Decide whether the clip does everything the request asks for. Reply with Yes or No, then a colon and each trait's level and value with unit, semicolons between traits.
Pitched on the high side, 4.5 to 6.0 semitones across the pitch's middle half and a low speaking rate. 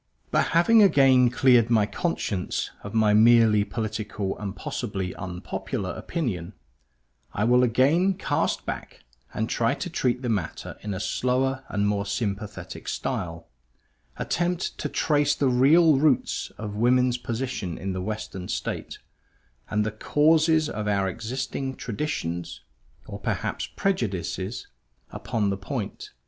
No: low, 115 Hz; average, 4.8 semitones; slow, 130 wpm